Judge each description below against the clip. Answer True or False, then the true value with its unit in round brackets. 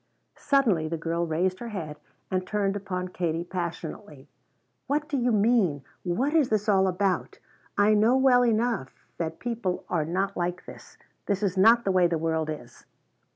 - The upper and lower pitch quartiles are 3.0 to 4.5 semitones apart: False (4.9 semitones)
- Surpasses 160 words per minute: True (170 wpm)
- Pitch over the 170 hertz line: True (190 Hz)